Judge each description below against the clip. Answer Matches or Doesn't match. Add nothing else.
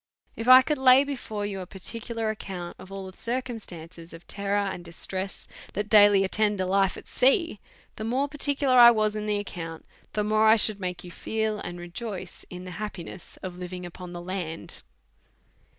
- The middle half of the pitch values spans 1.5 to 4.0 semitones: Matches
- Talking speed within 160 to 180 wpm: Doesn't match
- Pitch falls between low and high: Doesn't match